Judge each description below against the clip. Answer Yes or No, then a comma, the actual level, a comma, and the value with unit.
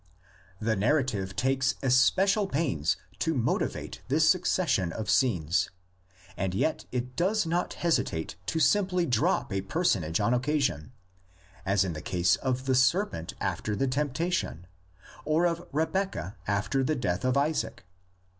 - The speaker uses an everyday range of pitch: No, wide, 8.6 semitones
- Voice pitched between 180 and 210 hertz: No, low, 130 Hz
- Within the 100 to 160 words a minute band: Yes, slow, 135 wpm